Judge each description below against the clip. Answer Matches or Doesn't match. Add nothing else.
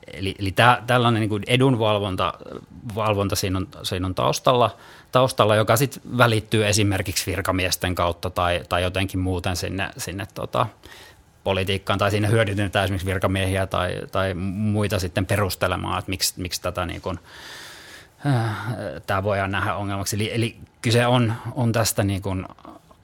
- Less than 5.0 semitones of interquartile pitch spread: Matches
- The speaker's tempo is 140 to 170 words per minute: Matches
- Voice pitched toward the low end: Matches